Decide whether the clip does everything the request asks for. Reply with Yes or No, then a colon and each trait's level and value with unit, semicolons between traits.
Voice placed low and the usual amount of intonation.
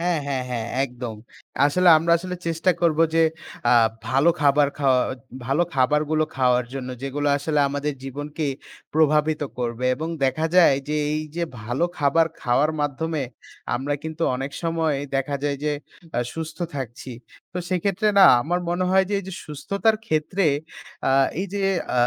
No: medium, 150 Hz; average, 3.5 semitones